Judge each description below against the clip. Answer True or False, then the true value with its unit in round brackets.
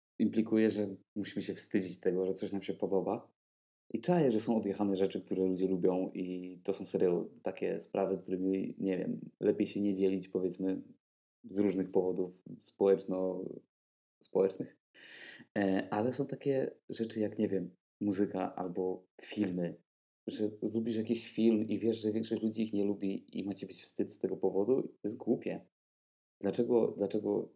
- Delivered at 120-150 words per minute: False (160 wpm)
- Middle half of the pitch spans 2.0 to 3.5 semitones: True (2.6 semitones)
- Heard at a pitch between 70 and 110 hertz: True (95 Hz)